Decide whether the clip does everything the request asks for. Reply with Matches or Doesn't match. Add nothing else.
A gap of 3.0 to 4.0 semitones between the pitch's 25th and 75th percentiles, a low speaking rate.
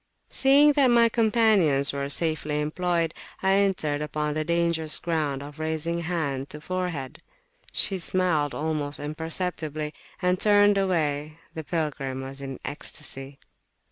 Matches